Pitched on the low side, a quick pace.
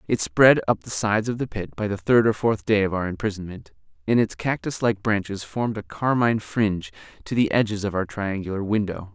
Yes: low, 105 Hz; fast, 215 wpm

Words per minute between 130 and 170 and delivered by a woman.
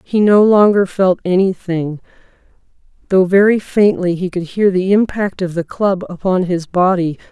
Yes: average, 155 wpm; female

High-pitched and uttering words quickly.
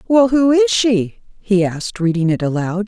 No: high, 200 Hz; average, 190 wpm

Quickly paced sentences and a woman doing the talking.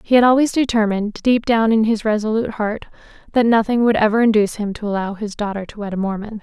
Yes: fast, 225 wpm; female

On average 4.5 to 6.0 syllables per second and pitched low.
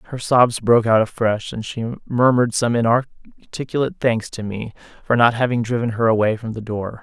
Yes: 5.5 syllables/s; low, 115 Hz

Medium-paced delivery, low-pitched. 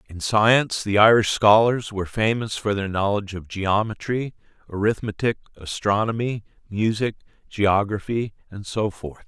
No: slow, 125 wpm; low, 105 Hz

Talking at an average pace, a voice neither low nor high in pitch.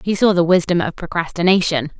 Yes: average, 180 wpm; medium, 175 Hz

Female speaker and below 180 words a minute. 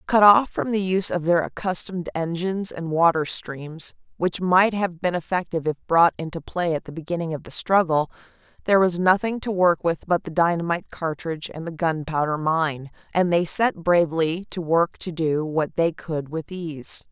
No: female; average, 190 wpm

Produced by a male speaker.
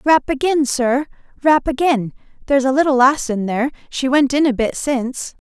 No: female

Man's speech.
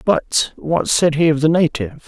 Yes: male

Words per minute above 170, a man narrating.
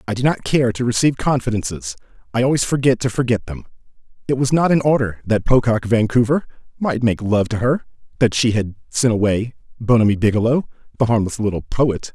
Yes: average, 180 wpm; male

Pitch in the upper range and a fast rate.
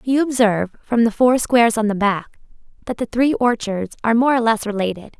Yes: high, 230 Hz; fast, 210 wpm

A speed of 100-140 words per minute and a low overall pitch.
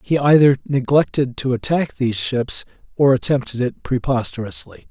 Yes: slow, 135 wpm; low, 130 Hz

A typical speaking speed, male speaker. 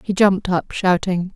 No: average, 175 wpm; female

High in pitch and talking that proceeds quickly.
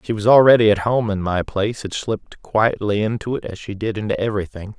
No: low, 105 Hz; fast, 225 wpm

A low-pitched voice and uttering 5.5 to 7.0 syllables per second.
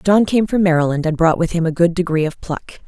No: medium, 170 Hz; 5.7 syllables/s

